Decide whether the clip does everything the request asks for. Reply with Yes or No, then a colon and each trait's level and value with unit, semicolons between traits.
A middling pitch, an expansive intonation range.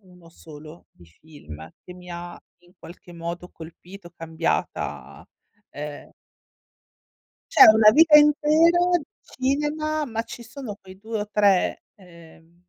Yes: medium, 180 Hz; wide, 7.4 semitones